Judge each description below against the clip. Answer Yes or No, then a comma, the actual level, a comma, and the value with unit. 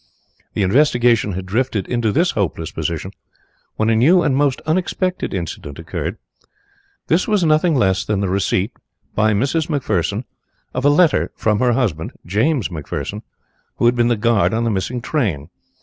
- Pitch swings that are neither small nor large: No, wide, 6.4 semitones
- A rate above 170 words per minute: No, average, 165 wpm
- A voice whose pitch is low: Yes, low, 120 Hz